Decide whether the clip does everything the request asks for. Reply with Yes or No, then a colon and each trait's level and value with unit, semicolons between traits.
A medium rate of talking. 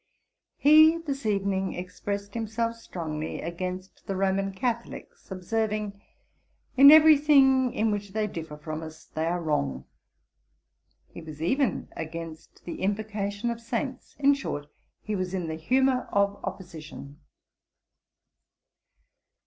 No: slow, 125 wpm